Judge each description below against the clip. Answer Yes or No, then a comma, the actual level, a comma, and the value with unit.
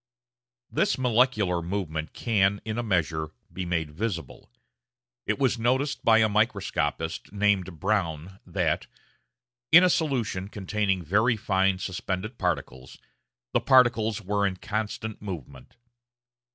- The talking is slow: Yes, slow, 120 wpm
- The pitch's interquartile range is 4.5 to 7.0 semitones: No, average, 3.8 semitones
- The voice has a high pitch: No, low, 100 Hz